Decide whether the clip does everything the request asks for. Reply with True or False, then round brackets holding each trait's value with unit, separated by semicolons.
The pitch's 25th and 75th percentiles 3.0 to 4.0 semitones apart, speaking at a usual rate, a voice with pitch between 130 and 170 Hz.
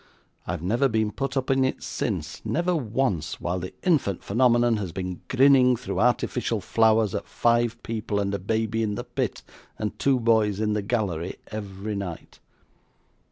False (3.7 semitones; 165 wpm; 110 Hz)